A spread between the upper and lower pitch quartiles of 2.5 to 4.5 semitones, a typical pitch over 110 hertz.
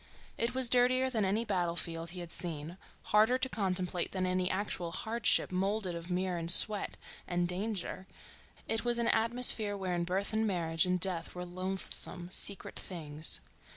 Yes: average, 3.8 semitones; medium, 185 Hz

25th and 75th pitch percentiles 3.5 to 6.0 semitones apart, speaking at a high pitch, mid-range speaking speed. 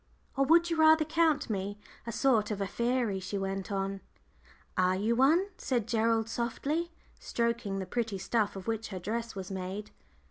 Yes: average, 4.9 semitones; high, 225 Hz; average, 180 wpm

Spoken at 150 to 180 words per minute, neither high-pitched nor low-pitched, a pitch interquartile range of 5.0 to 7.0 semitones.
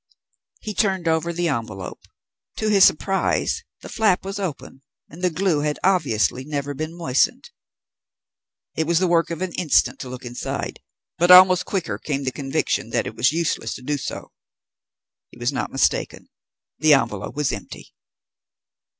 Yes: average, 160 wpm; medium, 155 Hz; average, 5.3 semitones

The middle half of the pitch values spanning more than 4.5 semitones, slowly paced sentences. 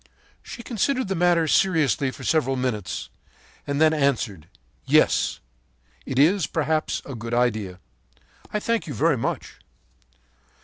Yes: wide, 5.6 semitones; slow, 130 wpm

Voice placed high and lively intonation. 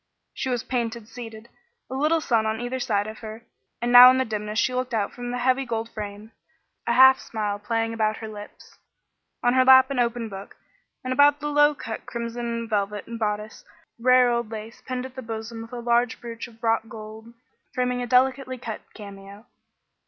No: high, 235 Hz; narrow, 2.5 semitones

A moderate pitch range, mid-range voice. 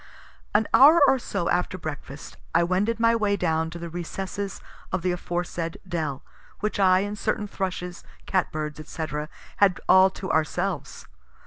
Yes: average, 3.2 semitones; medium, 180 Hz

